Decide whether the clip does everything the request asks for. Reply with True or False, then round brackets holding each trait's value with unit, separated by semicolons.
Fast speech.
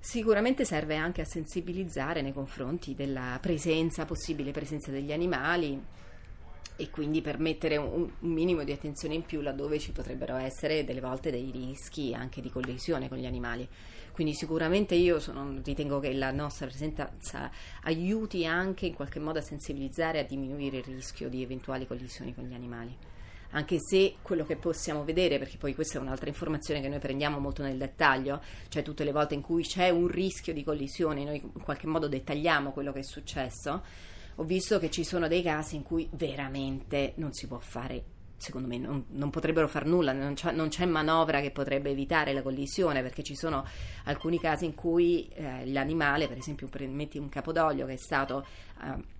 True (185 wpm)